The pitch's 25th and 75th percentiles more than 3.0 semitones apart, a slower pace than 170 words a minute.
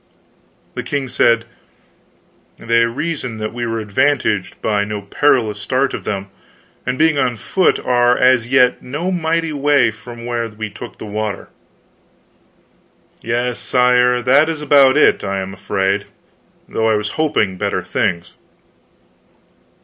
Yes: average, 4.3 semitones; average, 140 wpm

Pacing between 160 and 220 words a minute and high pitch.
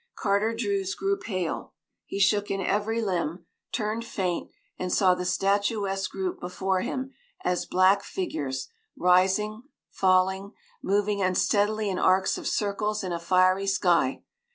No: slow, 135 wpm; high, 195 Hz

